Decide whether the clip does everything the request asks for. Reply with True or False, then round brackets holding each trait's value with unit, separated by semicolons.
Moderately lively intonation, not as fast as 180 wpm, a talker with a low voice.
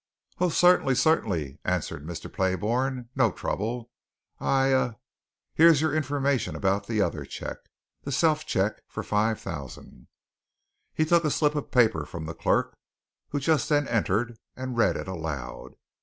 False (7.0 semitones; 150 wpm; 120 Hz)